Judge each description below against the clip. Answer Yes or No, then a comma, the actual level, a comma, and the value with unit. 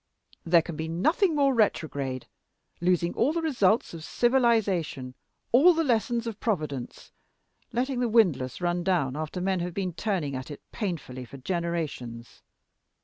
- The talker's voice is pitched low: No, medium, 180 Hz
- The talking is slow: No, average, 145 wpm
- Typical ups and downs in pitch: No, wide, 7.2 semitones